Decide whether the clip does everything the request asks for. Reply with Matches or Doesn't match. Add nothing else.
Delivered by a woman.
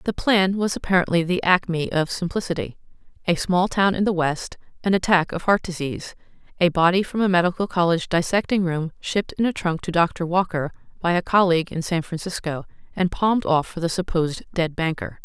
Matches